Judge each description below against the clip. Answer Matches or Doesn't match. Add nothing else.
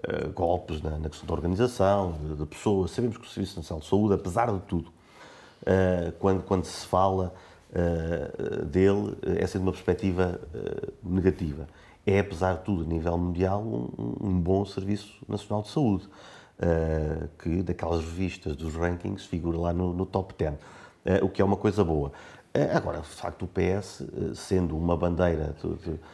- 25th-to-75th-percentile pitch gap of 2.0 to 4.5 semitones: Matches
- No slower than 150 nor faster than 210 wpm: Matches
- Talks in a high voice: Doesn't match